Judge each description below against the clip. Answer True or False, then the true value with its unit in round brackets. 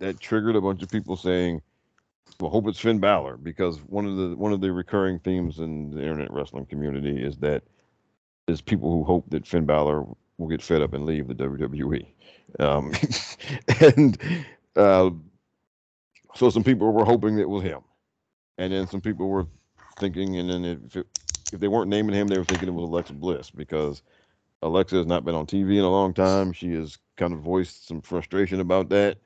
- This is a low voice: True (90 Hz)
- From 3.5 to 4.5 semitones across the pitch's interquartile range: True (3.9 semitones)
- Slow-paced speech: False (195 wpm)